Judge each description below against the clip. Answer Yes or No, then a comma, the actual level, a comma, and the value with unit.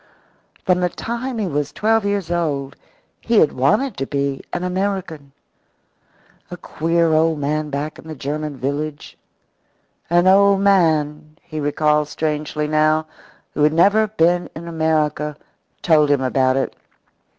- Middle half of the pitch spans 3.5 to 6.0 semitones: No, average, 3.1 semitones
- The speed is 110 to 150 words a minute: Yes, average, 140 wpm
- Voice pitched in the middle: Yes, medium, 155 Hz